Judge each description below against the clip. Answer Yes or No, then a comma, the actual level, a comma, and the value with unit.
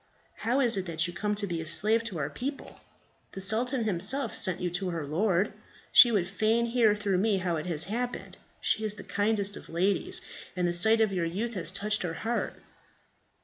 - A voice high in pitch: Yes, high, 200 Hz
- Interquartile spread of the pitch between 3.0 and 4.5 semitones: Yes, average, 4.1 semitones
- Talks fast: Yes, fast, 210 wpm